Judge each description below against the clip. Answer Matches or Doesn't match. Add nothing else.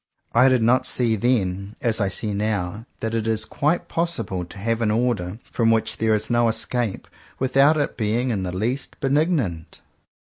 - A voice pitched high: Doesn't match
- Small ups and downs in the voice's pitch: Doesn't match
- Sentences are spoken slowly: Doesn't match